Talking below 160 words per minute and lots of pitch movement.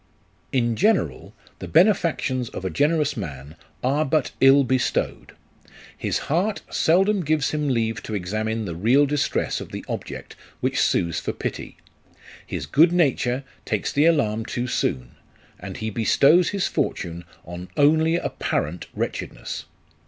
Yes: average, 140 wpm; wide, 6.7 semitones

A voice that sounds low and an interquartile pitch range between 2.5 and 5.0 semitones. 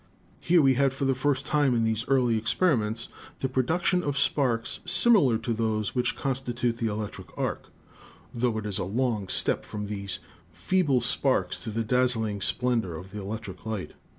Yes: low, 120 Hz; average, 3.8 semitones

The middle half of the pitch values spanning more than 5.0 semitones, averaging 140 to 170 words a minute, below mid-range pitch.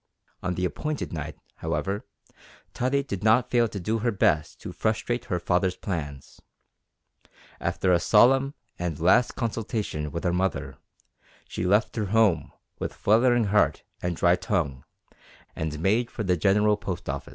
No: average, 4.4 semitones; average, 150 wpm; low, 100 Hz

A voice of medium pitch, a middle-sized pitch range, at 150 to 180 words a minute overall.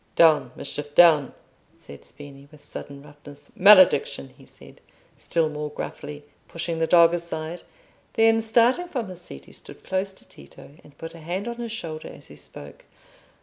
Yes: medium, 165 Hz; average, 4.6 semitones; average, 170 wpm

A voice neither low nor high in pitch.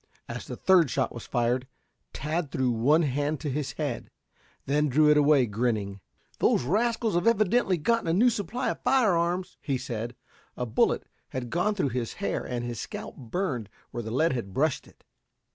Yes: medium, 145 Hz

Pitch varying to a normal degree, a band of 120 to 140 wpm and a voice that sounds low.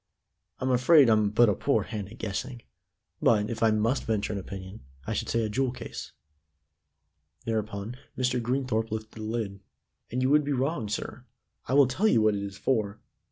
No: average, 3.3 semitones; average, 190 wpm; low, 115 Hz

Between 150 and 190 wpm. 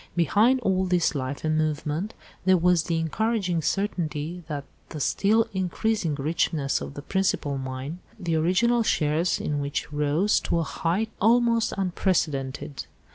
No: average, 140 wpm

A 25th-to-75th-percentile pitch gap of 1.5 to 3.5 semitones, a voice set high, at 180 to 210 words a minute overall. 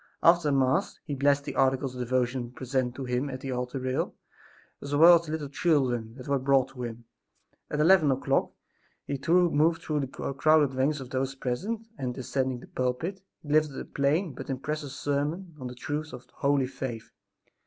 No: average, 2.8 semitones; low, 135 Hz; average, 185 wpm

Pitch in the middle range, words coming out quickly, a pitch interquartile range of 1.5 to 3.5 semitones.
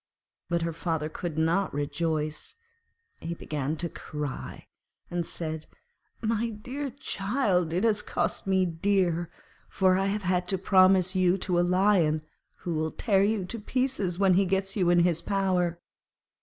No: medium, 180 Hz; average, 155 wpm; average, 2.8 semitones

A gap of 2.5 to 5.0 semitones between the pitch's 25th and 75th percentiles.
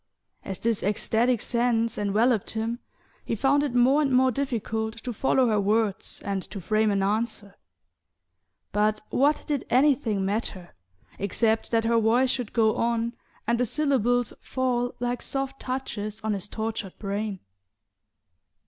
Yes: average, 2.9 semitones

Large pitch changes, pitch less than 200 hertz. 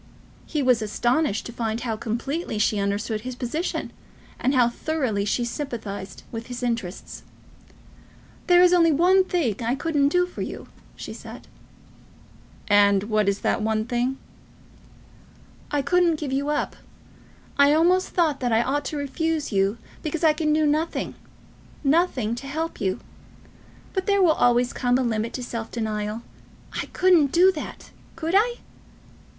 No: wide, 6.2 semitones; very high, 260 Hz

